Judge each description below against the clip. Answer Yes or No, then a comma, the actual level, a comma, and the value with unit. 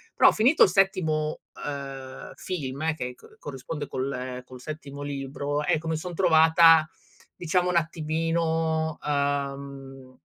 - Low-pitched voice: No, medium, 150 Hz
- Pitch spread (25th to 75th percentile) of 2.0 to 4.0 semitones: Yes, average, 2.9 semitones